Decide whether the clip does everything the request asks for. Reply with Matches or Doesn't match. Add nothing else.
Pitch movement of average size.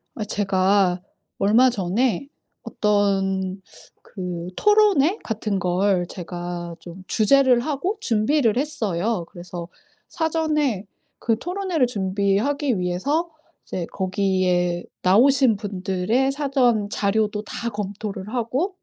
Doesn't match